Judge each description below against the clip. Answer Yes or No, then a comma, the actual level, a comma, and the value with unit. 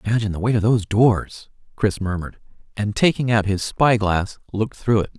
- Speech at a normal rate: Yes, average, 185 wpm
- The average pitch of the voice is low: Yes, low, 105 Hz